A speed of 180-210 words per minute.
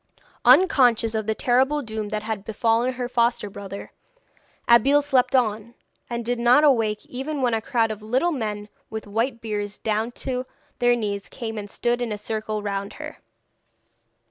No: average, 170 wpm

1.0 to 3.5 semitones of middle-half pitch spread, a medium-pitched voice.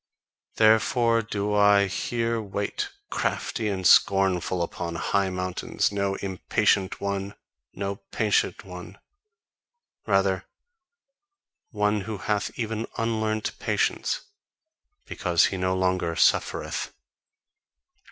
No: narrow, 2.5 semitones; low, 100 Hz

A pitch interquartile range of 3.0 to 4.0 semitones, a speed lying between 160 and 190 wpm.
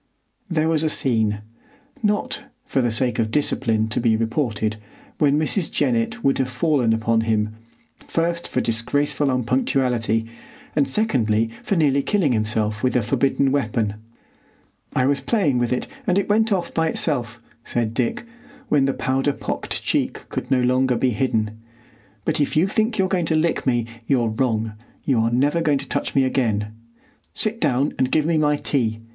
No: average, 5.3 semitones; average, 175 wpm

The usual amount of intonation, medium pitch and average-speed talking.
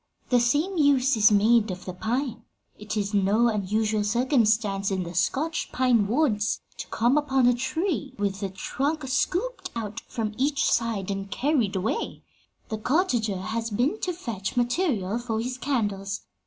No: average, 4.5 semitones; high, 230 Hz; average, 160 wpm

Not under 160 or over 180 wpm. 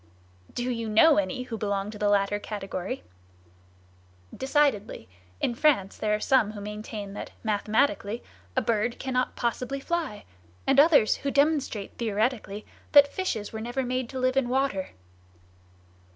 No: average, 145 wpm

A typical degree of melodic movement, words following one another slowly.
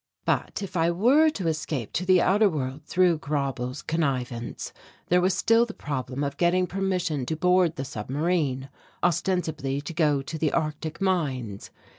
No: average, 4.8 semitones; average, 160 wpm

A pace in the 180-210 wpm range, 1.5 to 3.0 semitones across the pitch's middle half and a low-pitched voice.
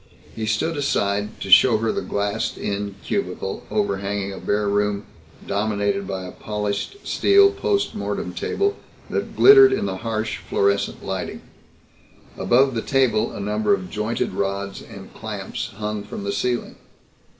No: average, 150 wpm; narrow, 2.4 semitones; low, 105 Hz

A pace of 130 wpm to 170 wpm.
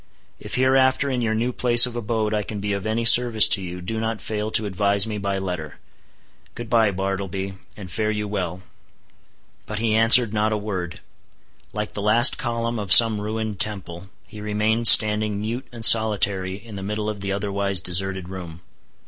No: average, 185 wpm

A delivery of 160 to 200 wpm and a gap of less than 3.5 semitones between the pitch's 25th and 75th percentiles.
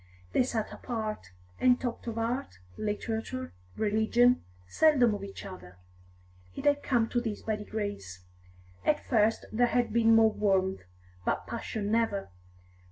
No: average, 140 wpm; average, 2.8 semitones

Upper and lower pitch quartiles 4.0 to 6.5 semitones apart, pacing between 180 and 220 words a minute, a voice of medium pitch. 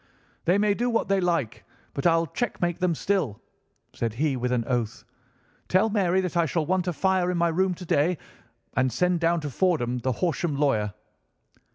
Yes: wide, 5.5 semitones; average, 190 wpm; medium, 170 Hz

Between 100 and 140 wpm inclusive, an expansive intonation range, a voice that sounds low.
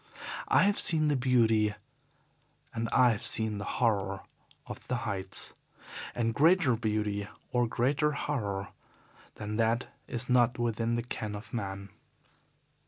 No: slow, 135 wpm; average, 3.2 semitones; low, 115 Hz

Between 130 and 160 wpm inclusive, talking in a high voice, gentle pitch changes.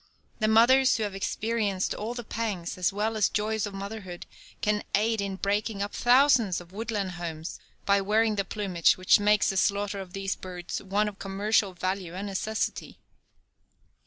No: average, 170 wpm; high, 205 Hz; narrow, 2.2 semitones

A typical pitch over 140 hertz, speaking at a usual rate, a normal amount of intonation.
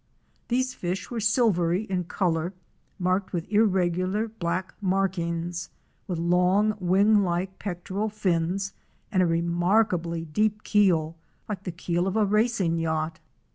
No: medium, 185 Hz; slow, 130 wpm; average, 3.2 semitones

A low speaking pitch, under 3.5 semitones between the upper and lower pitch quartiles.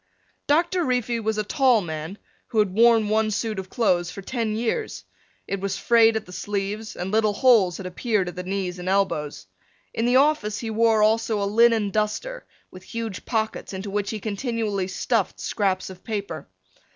No: high, 215 Hz; average, 3.0 semitones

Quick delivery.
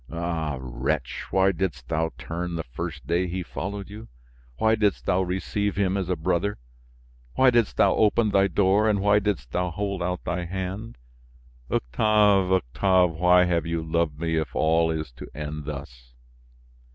No: average, 165 wpm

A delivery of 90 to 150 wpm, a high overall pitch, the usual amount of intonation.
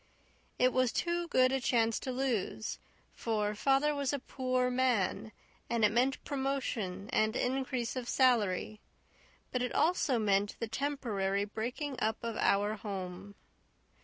Yes: average, 140 wpm; high, 240 Hz; average, 3.7 semitones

